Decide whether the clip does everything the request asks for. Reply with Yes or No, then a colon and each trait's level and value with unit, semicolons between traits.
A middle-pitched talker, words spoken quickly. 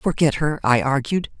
No: medium, 150 Hz; average, 170 wpm